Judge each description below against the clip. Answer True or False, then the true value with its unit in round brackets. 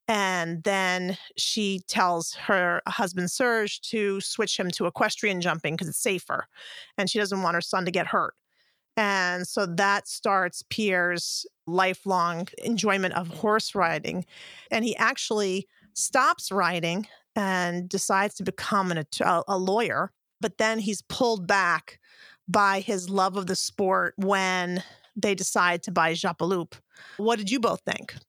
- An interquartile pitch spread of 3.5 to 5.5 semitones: False (2.9 semitones)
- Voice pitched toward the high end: True (195 Hz)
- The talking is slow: False (150 wpm)